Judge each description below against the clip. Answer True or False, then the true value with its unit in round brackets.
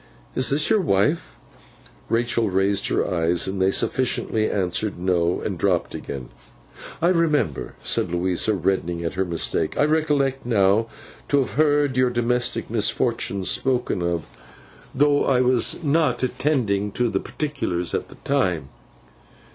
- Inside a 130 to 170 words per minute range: True (140 wpm)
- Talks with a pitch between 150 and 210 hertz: False (115 Hz)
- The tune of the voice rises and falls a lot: True (6.7 semitones)